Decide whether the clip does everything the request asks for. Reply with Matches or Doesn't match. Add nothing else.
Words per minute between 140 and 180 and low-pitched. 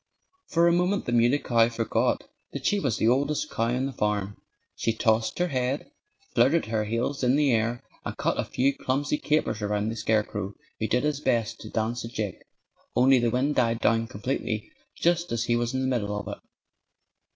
Doesn't match